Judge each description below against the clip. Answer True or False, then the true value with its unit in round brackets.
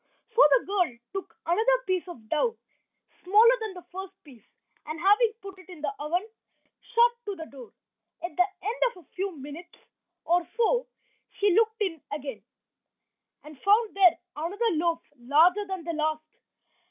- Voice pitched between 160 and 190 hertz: False (360 Hz)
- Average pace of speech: True (165 wpm)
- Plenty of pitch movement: False (5.0 semitones)